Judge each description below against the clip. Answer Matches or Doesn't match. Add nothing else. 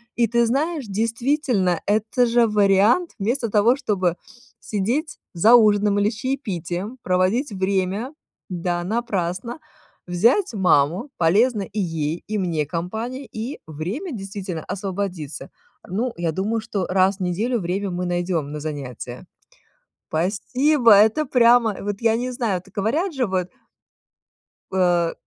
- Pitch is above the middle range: Matches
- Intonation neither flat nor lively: Matches